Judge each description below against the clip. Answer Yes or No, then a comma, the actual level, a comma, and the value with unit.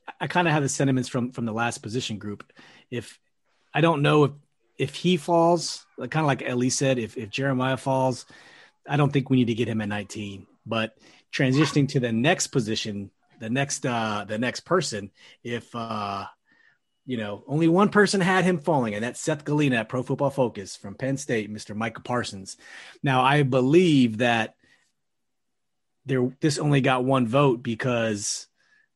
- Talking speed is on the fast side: No, average, 180 wpm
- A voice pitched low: Yes, low, 130 Hz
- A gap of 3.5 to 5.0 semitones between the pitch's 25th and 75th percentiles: Yes, average, 4.2 semitones